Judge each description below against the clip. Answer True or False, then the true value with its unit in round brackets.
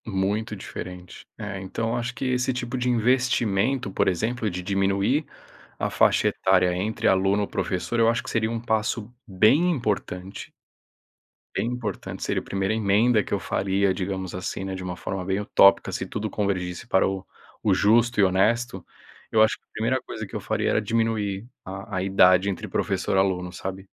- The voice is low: True (100 Hz)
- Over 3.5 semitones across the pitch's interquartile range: False (3.2 semitones)